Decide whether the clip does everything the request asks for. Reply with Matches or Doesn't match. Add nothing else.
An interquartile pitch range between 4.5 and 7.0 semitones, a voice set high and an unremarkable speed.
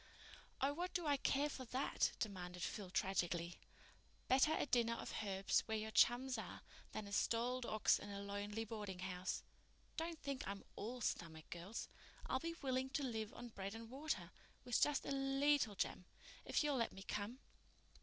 Matches